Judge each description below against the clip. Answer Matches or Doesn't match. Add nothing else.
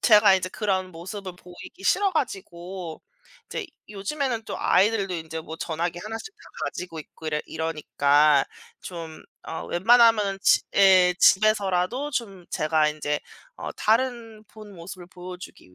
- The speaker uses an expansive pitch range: Doesn't match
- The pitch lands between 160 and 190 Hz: Matches